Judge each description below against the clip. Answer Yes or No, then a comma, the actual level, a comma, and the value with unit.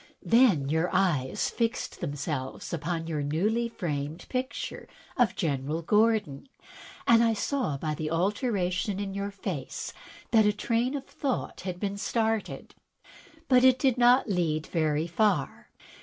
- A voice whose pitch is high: Yes, high, 195 Hz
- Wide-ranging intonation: Yes, wide, 6.4 semitones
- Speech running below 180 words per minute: Yes, average, 140 wpm